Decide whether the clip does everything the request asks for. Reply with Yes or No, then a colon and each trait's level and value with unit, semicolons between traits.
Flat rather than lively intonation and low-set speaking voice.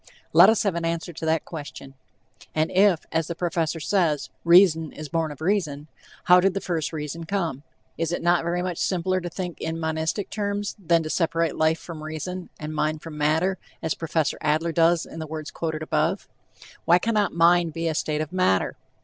No: narrow, 2.2 semitones; medium, 165 Hz